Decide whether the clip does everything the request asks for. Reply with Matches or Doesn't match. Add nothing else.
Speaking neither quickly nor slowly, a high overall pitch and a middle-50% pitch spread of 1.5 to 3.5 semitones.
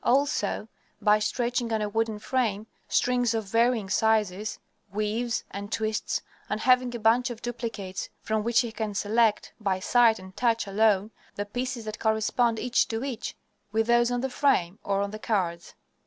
Matches